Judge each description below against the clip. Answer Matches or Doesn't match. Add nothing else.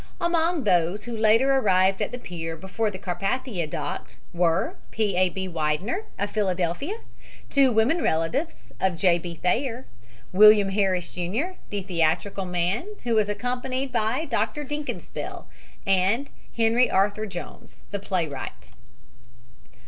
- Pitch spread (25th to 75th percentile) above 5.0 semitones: Matches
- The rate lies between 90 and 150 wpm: Matches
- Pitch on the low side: Doesn't match